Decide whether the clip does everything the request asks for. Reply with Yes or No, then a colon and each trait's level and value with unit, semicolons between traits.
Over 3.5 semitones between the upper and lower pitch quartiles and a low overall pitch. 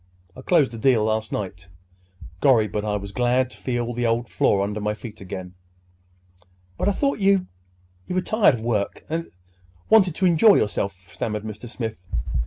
Yes: average, 4.9 semitones; low, 110 Hz